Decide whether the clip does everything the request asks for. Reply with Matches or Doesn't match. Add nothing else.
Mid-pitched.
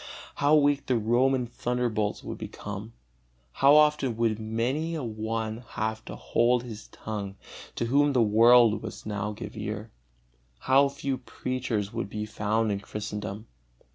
Doesn't match